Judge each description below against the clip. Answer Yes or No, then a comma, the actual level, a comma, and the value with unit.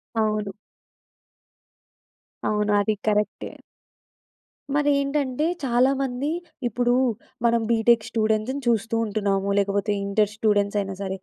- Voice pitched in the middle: No, high, 220 Hz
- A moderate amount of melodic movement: Yes, average, 3.2 semitones